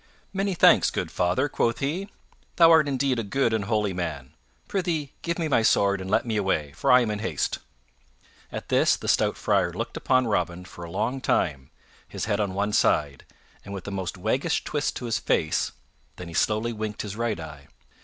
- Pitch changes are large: Yes, wide, 6.4 semitones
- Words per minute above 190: Yes, fast, 205 wpm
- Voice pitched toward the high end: No, low, 105 Hz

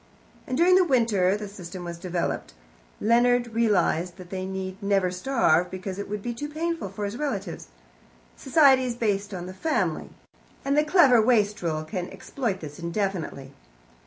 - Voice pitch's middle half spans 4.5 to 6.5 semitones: Yes, average, 5.2 semitones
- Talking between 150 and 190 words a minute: Yes, average, 160 wpm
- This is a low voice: No, high, 200 Hz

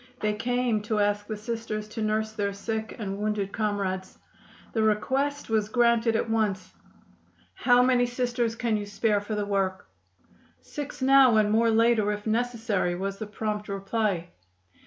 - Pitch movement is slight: Yes, narrow, 2.1 semitones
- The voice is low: No, high, 215 Hz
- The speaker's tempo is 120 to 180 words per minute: Yes, average, 155 wpm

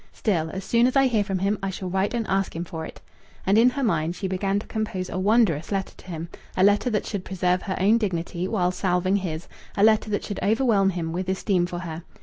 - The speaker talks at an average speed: No, fast, 245 wpm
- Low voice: No, high, 190 Hz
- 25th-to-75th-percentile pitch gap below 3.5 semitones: Yes, average, 2.8 semitones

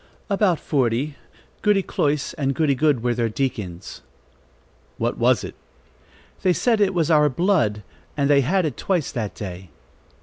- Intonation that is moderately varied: No, wide, 6.5 semitones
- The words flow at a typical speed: Yes, average, 155 wpm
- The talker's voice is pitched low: No, medium, 145 Hz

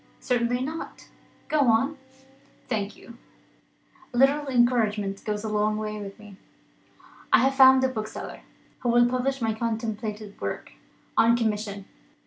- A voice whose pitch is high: Yes, high, 230 Hz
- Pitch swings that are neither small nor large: Yes, average, 3.2 semitones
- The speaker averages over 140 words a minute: No, slow, 135 wpm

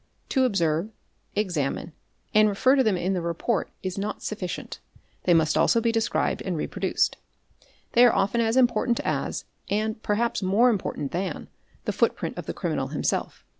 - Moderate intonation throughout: Yes, average, 4.5 semitones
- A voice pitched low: No, high, 210 Hz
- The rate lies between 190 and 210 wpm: No, average, 165 wpm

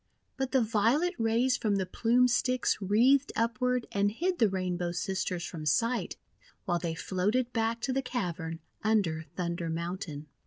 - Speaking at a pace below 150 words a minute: No, average, 155 wpm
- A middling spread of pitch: No, wide, 5.8 semitones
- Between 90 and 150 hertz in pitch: No, high, 215 Hz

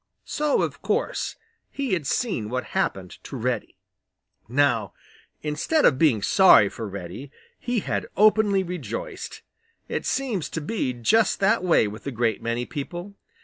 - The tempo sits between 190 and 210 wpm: No, average, 145 wpm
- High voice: No, medium, 155 Hz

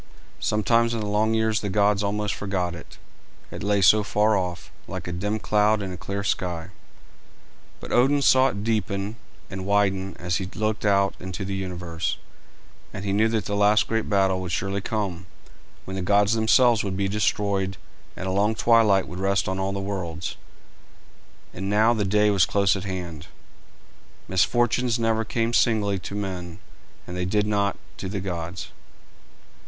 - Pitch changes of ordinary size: No, narrow, 2.2 semitones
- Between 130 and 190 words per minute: Yes, average, 175 wpm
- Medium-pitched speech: No, low, 100 Hz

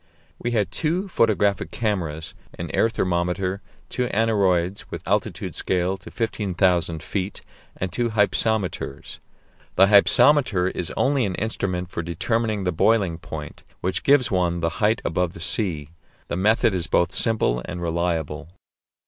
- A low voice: Yes, very low, 95 Hz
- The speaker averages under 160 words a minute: Yes, average, 140 wpm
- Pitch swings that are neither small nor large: Yes, average, 4.2 semitones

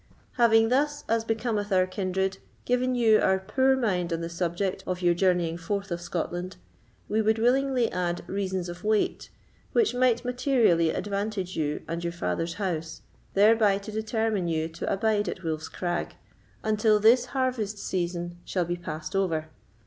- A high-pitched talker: Yes, high, 195 Hz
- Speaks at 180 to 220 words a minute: No, average, 160 wpm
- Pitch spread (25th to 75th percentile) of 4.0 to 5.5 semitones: Yes, average, 4.4 semitones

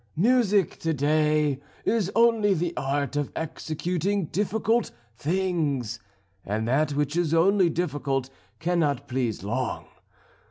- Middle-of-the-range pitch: Yes, medium, 155 Hz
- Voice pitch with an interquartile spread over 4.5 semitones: Yes, average, 5.1 semitones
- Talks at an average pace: No, slow, 115 wpm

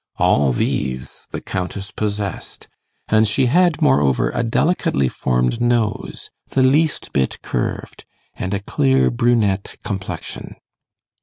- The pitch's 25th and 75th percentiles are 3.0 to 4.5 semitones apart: No, wide, 5.4 semitones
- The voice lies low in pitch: Yes, low, 105 Hz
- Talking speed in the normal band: No, slow, 120 wpm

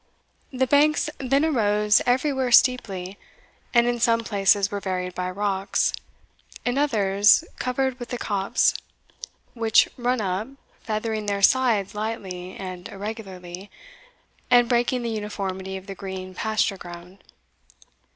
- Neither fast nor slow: No, slow, 125 wpm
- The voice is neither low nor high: No, high, 210 Hz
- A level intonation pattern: No, average, 4.1 semitones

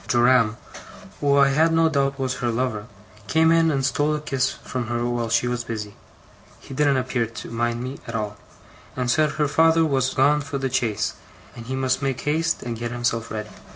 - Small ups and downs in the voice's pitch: No, average, 3.4 semitones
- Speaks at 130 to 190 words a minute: No, fast, 205 wpm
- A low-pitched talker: Yes, low, 130 Hz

